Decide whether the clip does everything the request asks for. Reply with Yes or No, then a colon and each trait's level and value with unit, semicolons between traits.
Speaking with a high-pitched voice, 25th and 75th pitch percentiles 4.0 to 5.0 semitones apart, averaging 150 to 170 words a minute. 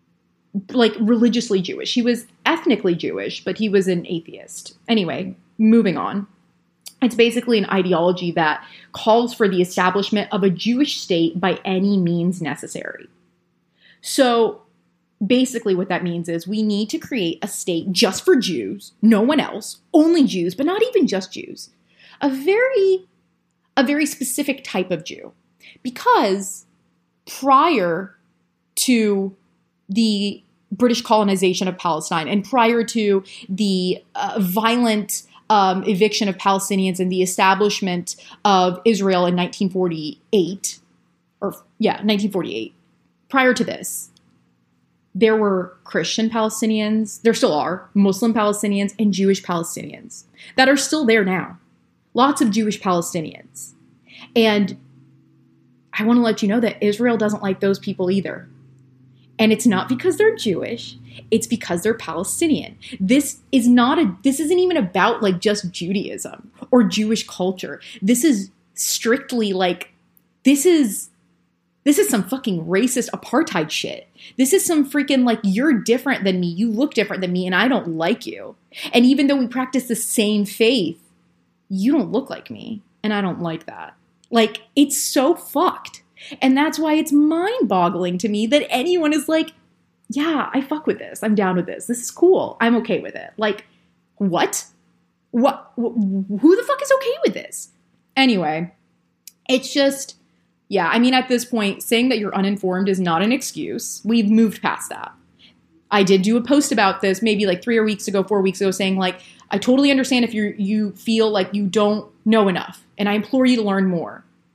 Yes: high, 215 Hz; average, 4.7 semitones; average, 160 wpm